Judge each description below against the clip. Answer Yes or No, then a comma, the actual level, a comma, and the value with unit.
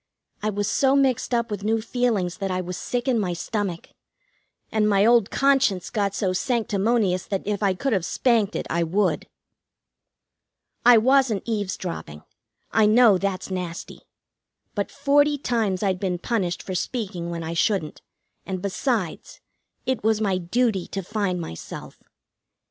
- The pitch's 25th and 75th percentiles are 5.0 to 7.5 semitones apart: No, average, 4.2 semitones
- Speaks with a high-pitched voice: Yes, high, 205 Hz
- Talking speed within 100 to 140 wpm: No, average, 155 wpm